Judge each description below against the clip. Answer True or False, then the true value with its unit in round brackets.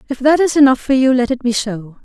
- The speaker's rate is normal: False (295 wpm)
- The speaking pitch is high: True (255 Hz)